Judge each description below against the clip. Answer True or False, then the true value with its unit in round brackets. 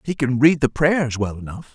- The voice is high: False (135 Hz)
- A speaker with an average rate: False (240 wpm)